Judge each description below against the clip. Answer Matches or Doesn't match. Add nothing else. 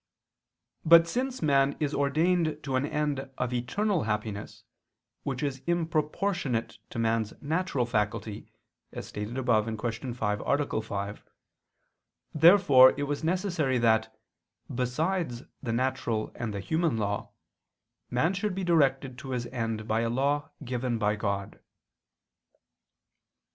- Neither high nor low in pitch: Doesn't match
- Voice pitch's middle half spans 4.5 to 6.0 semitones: Matches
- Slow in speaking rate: Matches